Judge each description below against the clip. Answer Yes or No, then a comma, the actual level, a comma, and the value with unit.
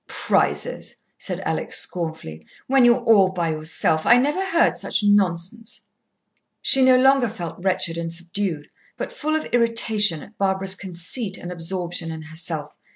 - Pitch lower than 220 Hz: Yes, high, 190 Hz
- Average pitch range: No, wide, 5.8 semitones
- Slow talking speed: No, average, 150 wpm